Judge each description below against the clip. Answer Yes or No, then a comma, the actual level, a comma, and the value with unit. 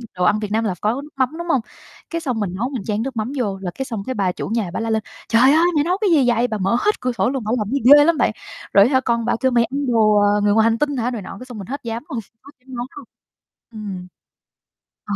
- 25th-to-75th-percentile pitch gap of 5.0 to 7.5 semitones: No, average, 4.1 semitones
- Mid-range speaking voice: No, high, 235 Hz